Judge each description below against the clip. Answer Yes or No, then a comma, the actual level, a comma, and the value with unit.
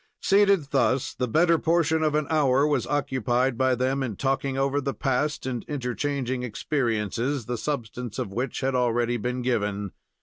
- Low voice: Yes, low, 130 Hz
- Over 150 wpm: Yes, average, 165 wpm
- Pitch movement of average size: Yes, average, 3.0 semitones